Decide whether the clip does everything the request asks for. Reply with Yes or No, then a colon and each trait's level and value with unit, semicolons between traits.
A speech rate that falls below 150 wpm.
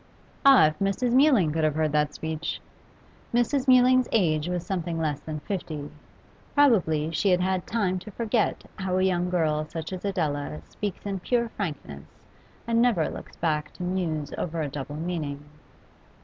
No: average, 165 wpm